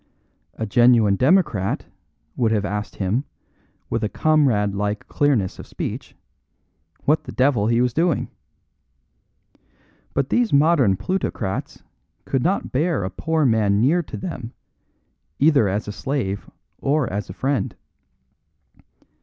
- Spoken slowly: Yes, slow, 125 wpm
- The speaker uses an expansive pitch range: Yes, wide, 6.1 semitones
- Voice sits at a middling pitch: No, low, 125 Hz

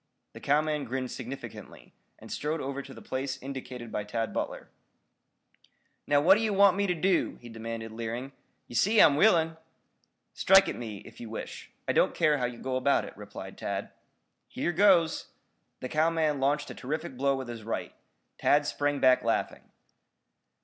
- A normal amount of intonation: Yes, average, 4.5 semitones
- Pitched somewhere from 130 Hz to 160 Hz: Yes, medium, 140 Hz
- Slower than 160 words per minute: No, average, 170 wpm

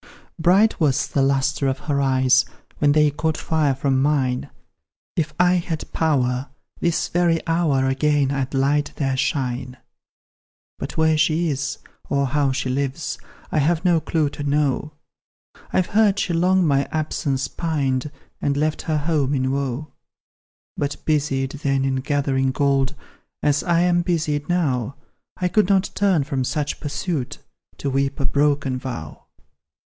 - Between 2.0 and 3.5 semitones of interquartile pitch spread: Yes, average, 3.0 semitones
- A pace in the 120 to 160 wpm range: Yes, average, 150 wpm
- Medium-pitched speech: Yes, medium, 145 Hz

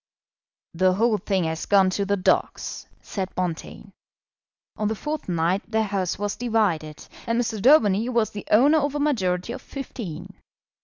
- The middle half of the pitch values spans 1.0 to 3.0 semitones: No, average, 4.2 semitones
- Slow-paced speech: No, average, 160 wpm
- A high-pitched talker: Yes, high, 205 Hz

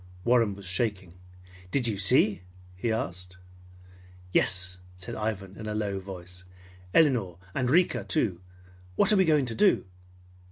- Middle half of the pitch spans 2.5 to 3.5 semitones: No, average, 5.0 semitones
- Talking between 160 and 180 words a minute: No, average, 145 wpm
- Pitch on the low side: Yes, low, 105 Hz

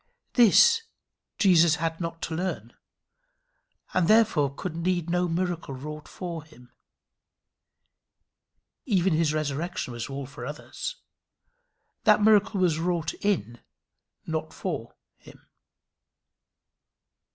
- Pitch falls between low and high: Yes, medium, 165 Hz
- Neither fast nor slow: No, slow, 105 wpm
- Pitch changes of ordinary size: Yes, average, 3.5 semitones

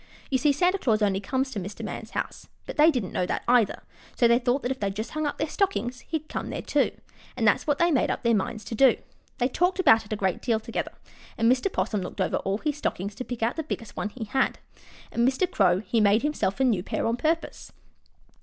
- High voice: Yes, high, 240 Hz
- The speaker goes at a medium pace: No, fast, 245 wpm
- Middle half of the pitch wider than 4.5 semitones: Yes, wide, 5.5 semitones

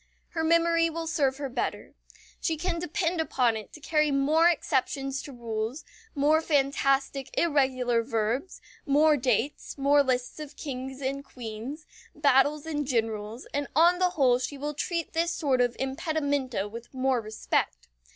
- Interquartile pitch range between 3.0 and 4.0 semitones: Yes, average, 3.6 semitones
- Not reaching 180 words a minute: Yes, average, 150 wpm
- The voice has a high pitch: Yes, very high, 275 Hz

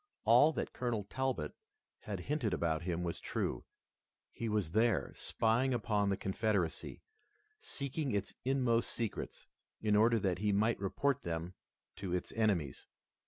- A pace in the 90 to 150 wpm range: Yes, average, 140 wpm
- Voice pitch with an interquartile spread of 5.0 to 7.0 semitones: No, average, 4.2 semitones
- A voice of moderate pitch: No, low, 110 Hz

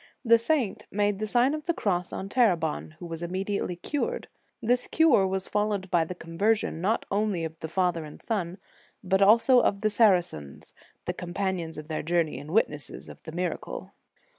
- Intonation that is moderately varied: Yes, average, 4.3 semitones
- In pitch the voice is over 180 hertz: Yes, high, 190 Hz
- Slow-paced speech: No, average, 185 wpm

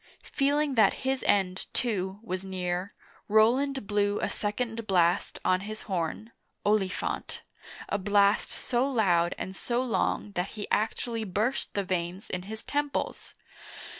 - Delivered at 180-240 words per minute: No, average, 155 wpm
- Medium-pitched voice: No, high, 205 Hz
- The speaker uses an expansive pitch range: No, average, 3.8 semitones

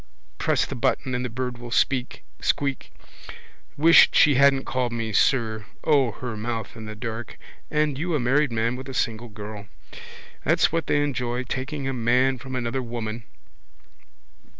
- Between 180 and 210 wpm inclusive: No, average, 160 wpm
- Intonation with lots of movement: No, average, 2.7 semitones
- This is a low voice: Yes, low, 125 Hz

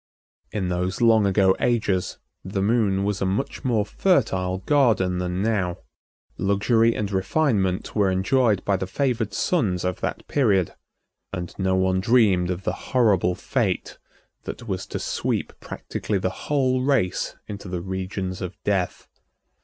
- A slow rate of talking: No, average, 145 wpm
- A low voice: Yes, low, 100 Hz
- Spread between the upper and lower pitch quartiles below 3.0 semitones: No, average, 3.5 semitones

